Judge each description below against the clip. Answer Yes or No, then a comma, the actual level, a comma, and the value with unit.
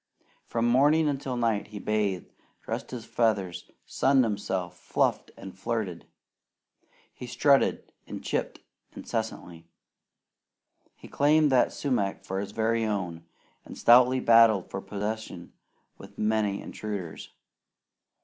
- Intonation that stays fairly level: No, average, 3.9 semitones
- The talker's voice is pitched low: Yes, low, 110 Hz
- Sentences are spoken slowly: Yes, slow, 115 wpm